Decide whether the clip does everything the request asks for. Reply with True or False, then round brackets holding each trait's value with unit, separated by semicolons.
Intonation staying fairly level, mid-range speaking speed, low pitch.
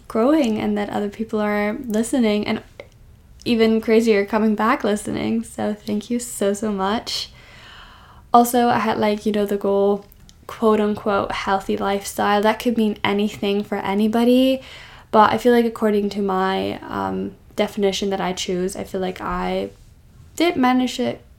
False (2.2 semitones; 155 wpm; 210 Hz)